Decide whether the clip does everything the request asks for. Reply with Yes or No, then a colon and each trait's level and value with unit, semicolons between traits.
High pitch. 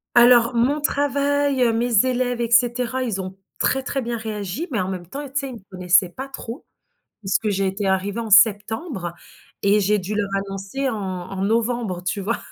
Yes: high, 225 Hz